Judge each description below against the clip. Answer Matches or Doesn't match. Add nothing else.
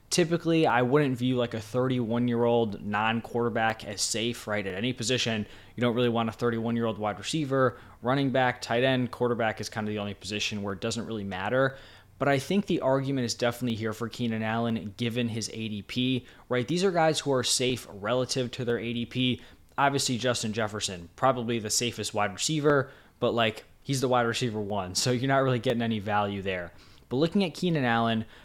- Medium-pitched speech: Doesn't match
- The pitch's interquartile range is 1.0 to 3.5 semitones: Matches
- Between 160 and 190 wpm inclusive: Doesn't match